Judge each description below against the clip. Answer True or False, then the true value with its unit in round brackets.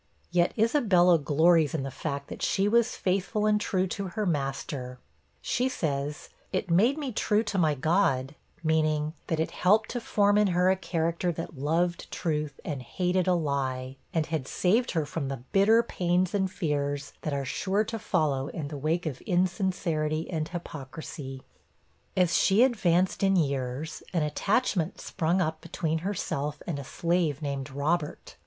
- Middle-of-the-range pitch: True (165 Hz)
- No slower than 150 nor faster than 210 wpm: True (165 wpm)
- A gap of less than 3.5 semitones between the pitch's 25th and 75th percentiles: False (4.3 semitones)